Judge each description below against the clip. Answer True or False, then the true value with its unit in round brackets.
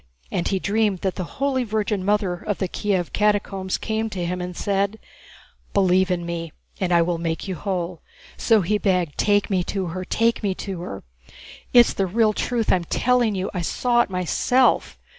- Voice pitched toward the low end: False (195 Hz)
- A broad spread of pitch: False (3.0 semitones)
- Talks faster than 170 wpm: True (190 wpm)